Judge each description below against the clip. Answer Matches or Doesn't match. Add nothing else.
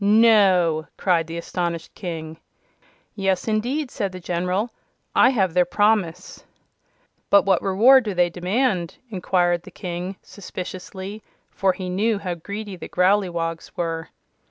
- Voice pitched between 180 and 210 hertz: Matches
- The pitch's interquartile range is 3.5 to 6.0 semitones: Doesn't match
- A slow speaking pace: Matches